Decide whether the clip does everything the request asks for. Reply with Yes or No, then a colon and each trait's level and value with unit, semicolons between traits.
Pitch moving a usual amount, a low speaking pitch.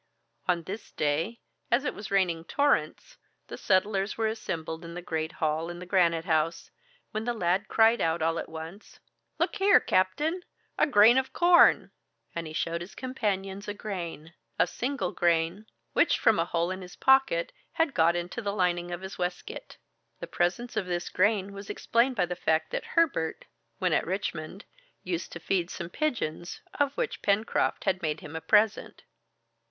No: average, 4.6 semitones; medium, 185 Hz